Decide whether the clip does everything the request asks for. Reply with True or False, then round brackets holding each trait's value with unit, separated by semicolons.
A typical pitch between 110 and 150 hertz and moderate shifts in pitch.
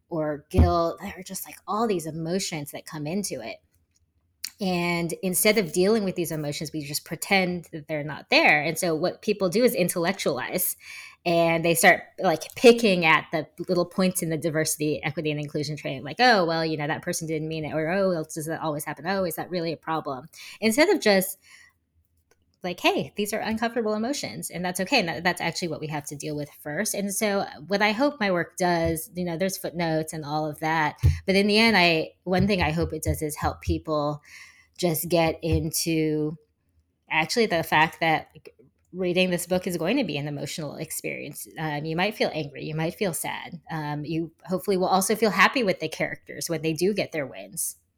False (165 Hz; 3.5 semitones)